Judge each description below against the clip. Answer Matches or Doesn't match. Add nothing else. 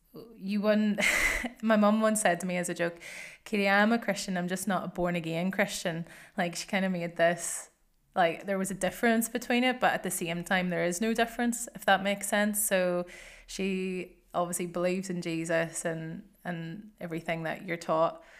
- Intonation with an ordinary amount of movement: Matches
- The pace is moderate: Matches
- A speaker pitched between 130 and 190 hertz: Matches